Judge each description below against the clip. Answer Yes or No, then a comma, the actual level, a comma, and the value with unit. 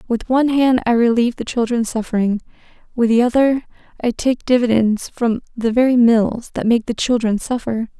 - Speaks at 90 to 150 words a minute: No, average, 175 wpm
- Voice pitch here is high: Yes, high, 235 Hz